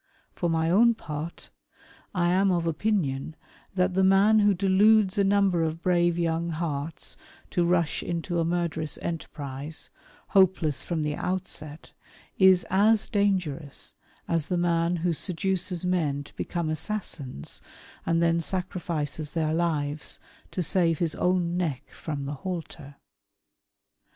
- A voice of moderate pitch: Yes, medium, 170 Hz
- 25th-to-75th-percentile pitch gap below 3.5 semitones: Yes, average, 2.9 semitones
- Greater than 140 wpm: No, slow, 135 wpm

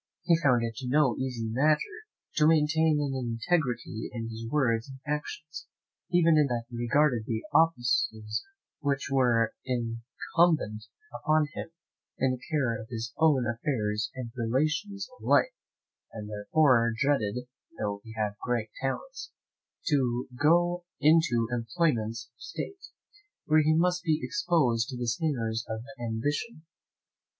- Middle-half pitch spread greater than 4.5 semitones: Yes, average, 5.1 semitones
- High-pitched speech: No, low, 130 Hz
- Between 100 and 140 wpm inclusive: Yes, slow, 135 wpm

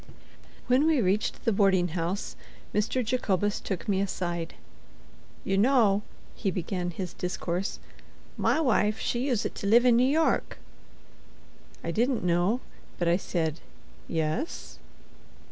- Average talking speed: No, slow, 130 wpm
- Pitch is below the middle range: No, high, 200 Hz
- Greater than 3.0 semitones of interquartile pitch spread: Yes, average, 5.3 semitones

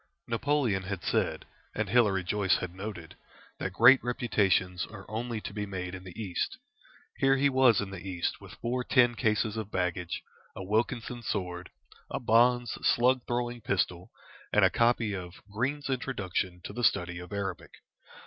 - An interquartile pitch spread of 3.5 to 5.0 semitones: Yes, average, 4.6 semitones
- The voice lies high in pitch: No, low, 105 Hz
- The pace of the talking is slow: No, average, 165 wpm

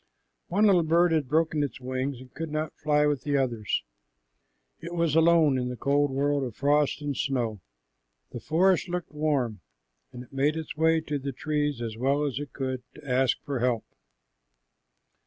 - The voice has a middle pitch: Yes, medium, 145 Hz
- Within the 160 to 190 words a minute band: Yes, average, 180 wpm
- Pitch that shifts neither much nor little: Yes, average, 3.3 semitones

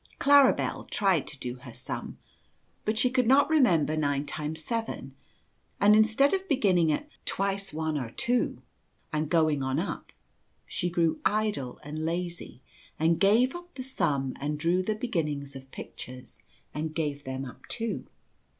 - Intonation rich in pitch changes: Yes, wide, 6.8 semitones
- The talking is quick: No, average, 160 wpm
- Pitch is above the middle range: No, medium, 165 Hz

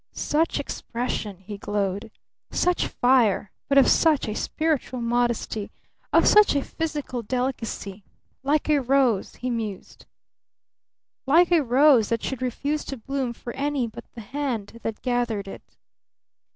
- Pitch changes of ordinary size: Yes, average, 4.1 semitones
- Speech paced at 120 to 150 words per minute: Yes, average, 140 wpm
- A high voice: Yes, high, 245 Hz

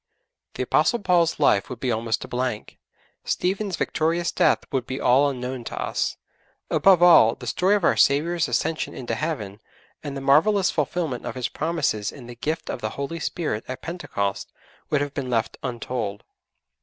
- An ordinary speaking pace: Yes, average, 175 wpm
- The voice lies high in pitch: No, medium, 140 Hz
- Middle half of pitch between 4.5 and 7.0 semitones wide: Yes, wide, 5.5 semitones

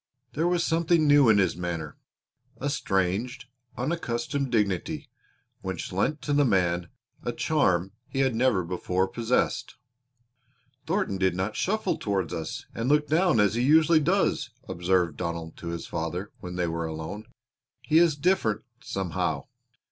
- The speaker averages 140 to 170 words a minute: Yes, average, 150 wpm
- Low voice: Yes, low, 105 Hz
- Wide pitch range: Yes, wide, 8.4 semitones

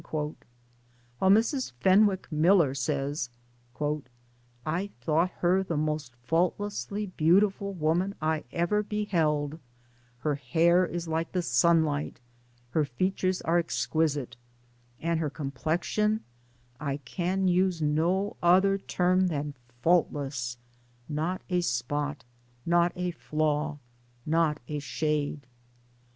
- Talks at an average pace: No, slow, 110 wpm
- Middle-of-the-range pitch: Yes, medium, 165 Hz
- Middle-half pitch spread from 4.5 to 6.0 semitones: No, average, 3.7 semitones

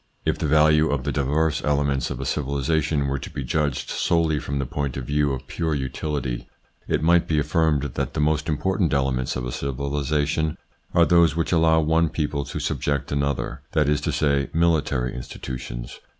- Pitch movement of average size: No, narrow, 2.3 semitones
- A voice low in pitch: Yes, very low, 75 Hz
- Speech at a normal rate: Yes, average, 185 wpm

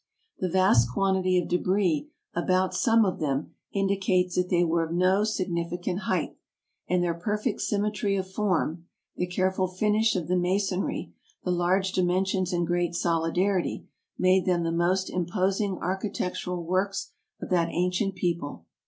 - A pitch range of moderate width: No, narrow, 1.8 semitones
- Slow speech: No, average, 145 wpm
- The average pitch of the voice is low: No, medium, 185 Hz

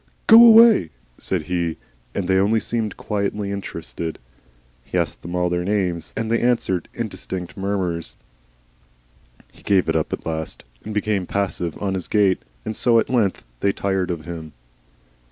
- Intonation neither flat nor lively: Yes, average, 3.2 semitones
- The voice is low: Yes, very low, 95 Hz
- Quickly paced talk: No, average, 165 wpm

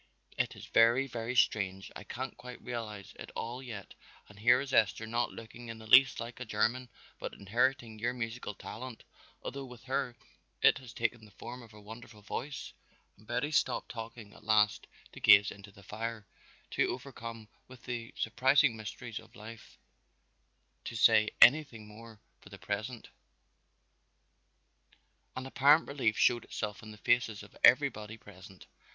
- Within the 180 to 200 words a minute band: No, average, 160 wpm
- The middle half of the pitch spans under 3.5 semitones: Yes, narrow, 2.6 semitones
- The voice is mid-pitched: No, low, 115 Hz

